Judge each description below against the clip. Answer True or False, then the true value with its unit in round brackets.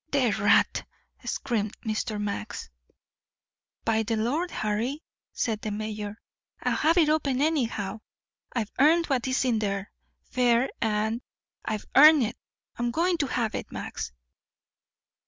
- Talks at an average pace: False (130 wpm)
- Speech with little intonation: False (4.5 semitones)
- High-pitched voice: True (235 Hz)